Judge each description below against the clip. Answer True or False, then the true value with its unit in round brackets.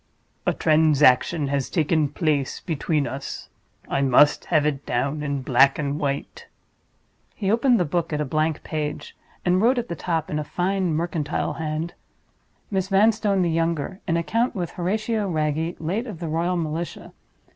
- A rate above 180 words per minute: False (165 wpm)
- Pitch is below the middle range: False (160 Hz)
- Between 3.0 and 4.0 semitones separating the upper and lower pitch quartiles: True (3.6 semitones)